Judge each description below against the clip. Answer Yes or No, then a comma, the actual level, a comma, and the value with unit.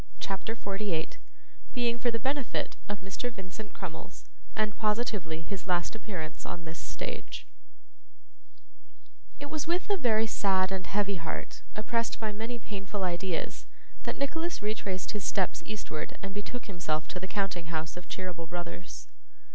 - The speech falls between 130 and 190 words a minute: Yes, average, 145 wpm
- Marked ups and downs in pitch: No, average, 4.0 semitones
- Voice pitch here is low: No, high, 200 Hz